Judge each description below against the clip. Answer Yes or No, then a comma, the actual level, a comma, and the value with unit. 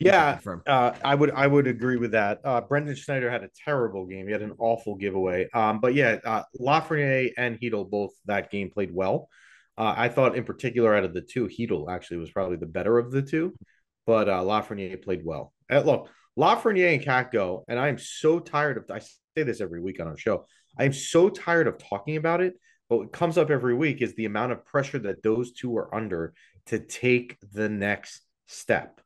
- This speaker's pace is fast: Yes, fast, 215 wpm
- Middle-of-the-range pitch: No, low, 120 Hz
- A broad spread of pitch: Yes, wide, 5.8 semitones